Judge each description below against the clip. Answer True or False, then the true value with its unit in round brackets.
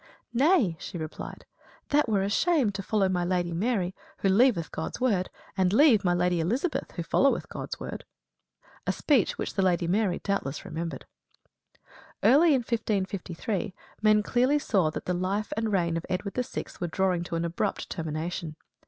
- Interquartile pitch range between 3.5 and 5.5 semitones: True (4.4 semitones)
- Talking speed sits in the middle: True (170 wpm)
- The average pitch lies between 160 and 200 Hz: True (190 Hz)